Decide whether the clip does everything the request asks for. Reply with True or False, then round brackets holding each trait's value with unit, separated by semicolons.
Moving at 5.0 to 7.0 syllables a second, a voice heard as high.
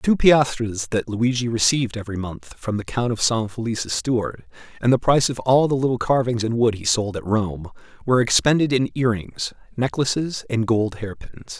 False (5.4 syllables/s; 115 Hz)